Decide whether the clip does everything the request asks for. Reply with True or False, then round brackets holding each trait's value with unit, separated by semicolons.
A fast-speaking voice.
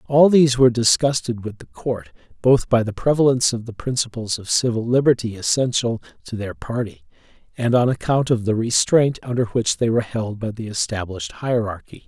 False (180 wpm)